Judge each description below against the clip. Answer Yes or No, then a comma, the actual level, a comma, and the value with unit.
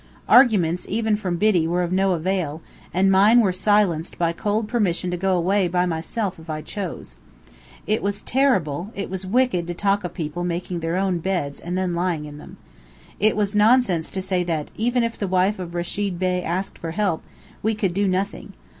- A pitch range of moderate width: Yes, average, 3.0 semitones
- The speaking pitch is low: No, medium, 185 Hz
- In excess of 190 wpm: Yes, average, 200 wpm